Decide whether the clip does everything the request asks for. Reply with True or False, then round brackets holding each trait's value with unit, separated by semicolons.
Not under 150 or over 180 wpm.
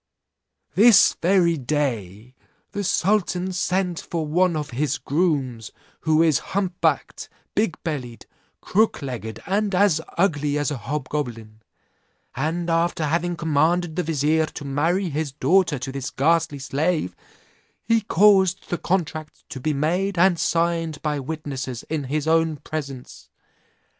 False (135 wpm)